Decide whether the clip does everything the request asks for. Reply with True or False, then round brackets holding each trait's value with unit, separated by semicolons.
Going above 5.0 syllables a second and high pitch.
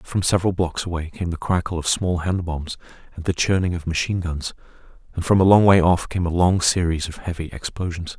False (5.7 syllables/s; 85 Hz)